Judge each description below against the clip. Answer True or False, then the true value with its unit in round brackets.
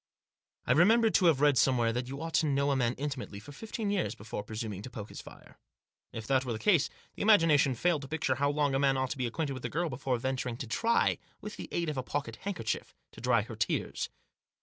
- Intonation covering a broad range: False (4.8 semitones)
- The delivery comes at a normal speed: False (240 wpm)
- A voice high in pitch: False (135 Hz)